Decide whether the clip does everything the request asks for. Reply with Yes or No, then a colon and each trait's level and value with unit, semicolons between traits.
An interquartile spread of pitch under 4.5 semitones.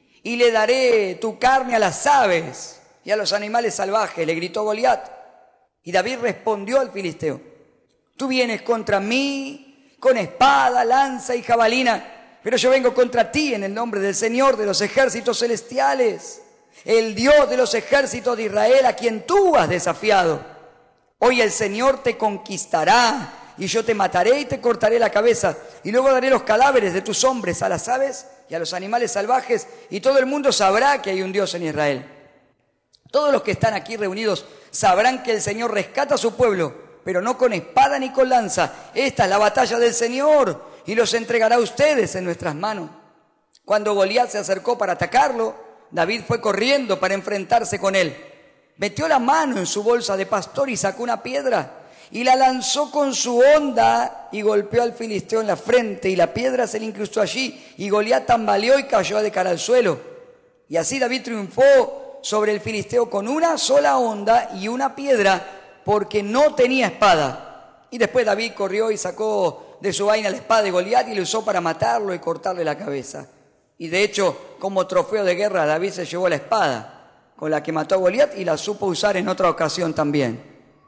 No: average, 4.9 semitones